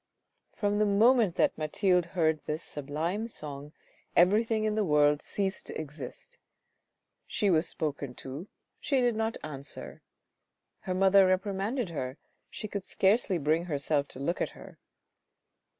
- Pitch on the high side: No, medium, 180 Hz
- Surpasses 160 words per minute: No, average, 140 wpm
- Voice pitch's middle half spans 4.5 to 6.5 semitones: Yes, wide, 5.6 semitones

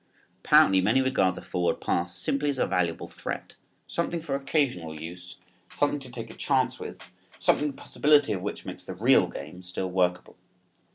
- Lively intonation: Yes, wide, 7.5 semitones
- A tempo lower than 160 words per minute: No, average, 175 wpm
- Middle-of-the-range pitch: No, low, 100 Hz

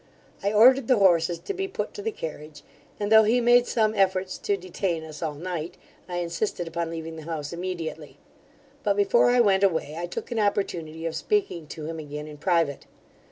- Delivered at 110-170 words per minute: No, average, 200 wpm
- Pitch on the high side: No, medium, 175 Hz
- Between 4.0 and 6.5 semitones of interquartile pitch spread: Yes, average, 4.6 semitones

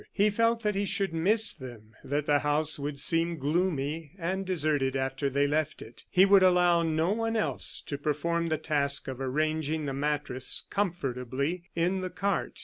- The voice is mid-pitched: Yes, medium, 155 Hz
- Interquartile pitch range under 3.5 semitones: No, average, 4.5 semitones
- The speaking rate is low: No, average, 175 wpm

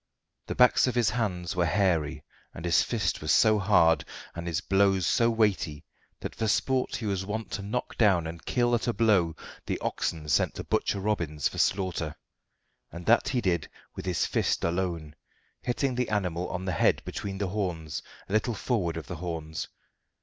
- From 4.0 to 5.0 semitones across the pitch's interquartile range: Yes, average, 4.6 semitones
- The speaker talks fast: No, average, 185 wpm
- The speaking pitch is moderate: No, very low, 95 Hz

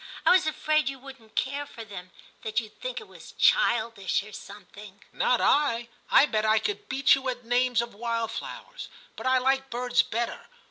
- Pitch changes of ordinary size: Yes, average, 3.7 semitones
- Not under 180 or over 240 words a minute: Yes, average, 195 wpm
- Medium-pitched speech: No, high, 245 Hz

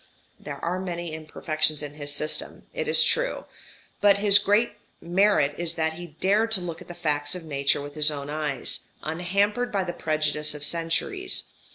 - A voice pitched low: No, medium, 165 Hz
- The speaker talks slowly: No, average, 180 wpm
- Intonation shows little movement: No, average, 3.9 semitones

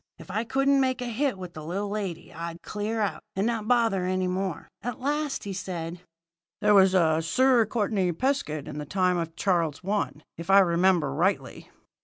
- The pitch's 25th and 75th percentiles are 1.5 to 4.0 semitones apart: No, average, 4.8 semitones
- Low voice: No, high, 195 Hz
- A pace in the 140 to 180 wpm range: No, average, 190 wpm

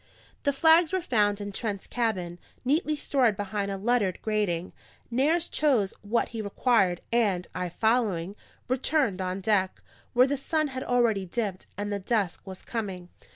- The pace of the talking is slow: No, average, 155 wpm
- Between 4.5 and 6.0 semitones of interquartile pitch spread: Yes, average, 4.8 semitones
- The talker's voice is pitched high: Yes, high, 215 Hz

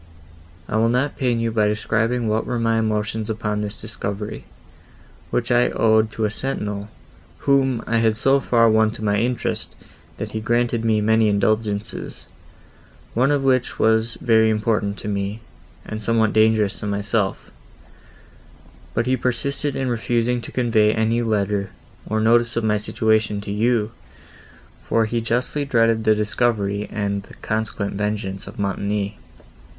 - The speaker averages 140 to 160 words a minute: Yes, average, 155 wpm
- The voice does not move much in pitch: Yes, narrow, 1.9 semitones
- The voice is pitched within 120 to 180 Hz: No, low, 110 Hz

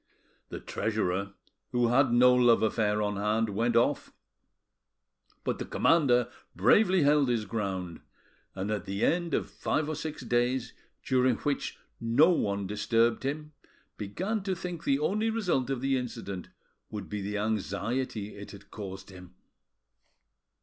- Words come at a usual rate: Yes, average, 145 wpm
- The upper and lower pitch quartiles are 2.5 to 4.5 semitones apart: No, average, 5.3 semitones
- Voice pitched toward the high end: No, low, 120 Hz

